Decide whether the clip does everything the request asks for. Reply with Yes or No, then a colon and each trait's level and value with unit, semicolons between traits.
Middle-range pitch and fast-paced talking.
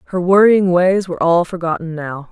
No: medium, 175 Hz; average, 180 wpm